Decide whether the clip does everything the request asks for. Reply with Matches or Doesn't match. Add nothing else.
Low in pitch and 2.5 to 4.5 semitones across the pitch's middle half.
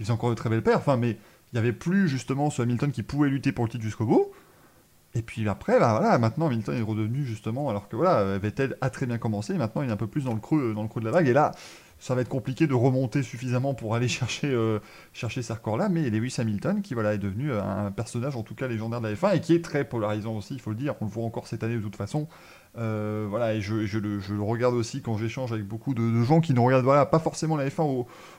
Matches